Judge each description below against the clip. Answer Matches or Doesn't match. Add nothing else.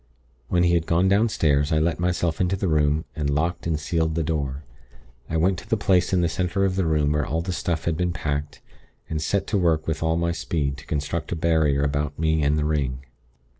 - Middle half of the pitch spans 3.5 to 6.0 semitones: Doesn't match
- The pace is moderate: Doesn't match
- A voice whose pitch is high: Doesn't match